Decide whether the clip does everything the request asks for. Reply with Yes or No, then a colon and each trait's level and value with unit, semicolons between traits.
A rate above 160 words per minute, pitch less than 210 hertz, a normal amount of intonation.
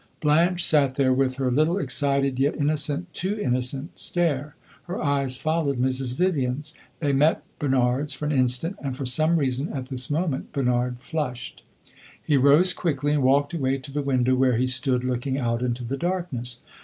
Yes: average, 175 wpm; medium, 140 Hz; average, 3.0 semitones